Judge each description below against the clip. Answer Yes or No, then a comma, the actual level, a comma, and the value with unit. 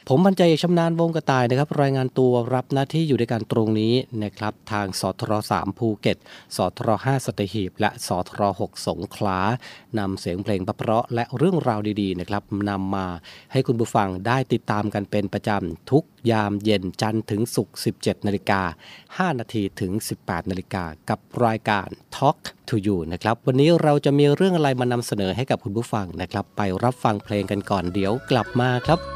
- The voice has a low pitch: Yes, low, 110 Hz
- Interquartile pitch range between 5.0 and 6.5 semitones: No, average, 4.1 semitones